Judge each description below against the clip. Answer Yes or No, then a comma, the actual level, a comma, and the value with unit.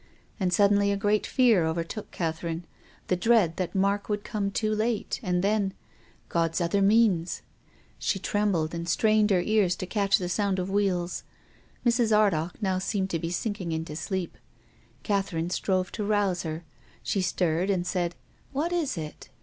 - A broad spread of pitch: No, average, 3.2 semitones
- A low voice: No, high, 190 Hz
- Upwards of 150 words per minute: Yes, average, 175 wpm